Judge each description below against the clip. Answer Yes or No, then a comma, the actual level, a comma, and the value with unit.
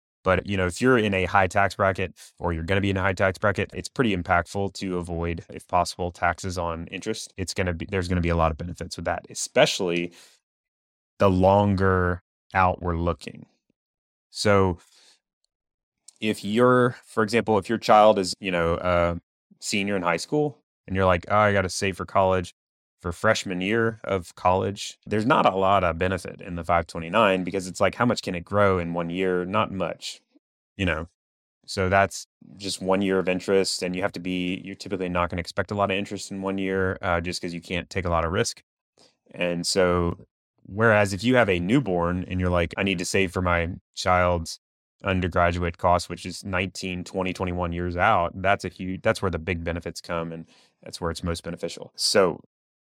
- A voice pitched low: Yes, very low, 95 Hz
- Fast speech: Yes, fast, 210 wpm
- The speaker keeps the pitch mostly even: Yes, narrow, 2.2 semitones